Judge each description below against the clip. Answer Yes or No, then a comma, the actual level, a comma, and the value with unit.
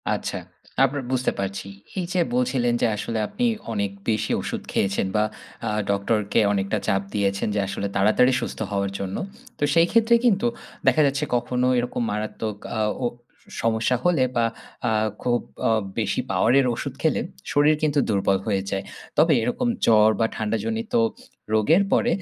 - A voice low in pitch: Yes, low, 115 Hz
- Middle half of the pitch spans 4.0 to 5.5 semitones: Yes, average, 5.2 semitones